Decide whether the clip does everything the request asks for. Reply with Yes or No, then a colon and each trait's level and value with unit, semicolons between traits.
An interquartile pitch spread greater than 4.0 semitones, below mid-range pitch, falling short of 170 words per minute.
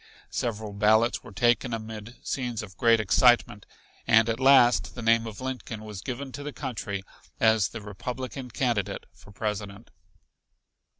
No: average, 2.9 semitones; low, 115 Hz; average, 145 wpm